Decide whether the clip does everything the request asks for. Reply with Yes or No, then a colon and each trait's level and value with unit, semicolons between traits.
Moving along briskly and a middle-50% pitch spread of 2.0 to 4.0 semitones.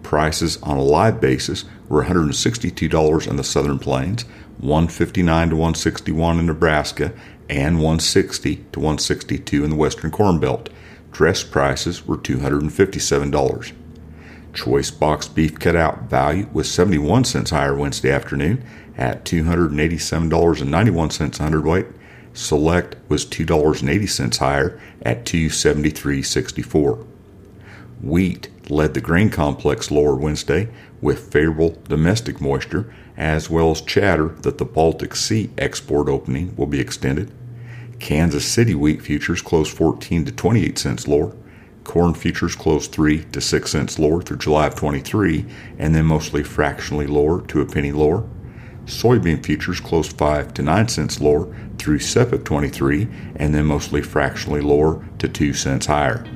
No: slow, 135 wpm; average, 3.3 semitones